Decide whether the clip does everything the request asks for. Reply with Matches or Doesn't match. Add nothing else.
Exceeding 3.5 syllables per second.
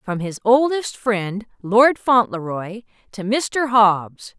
Doesn't match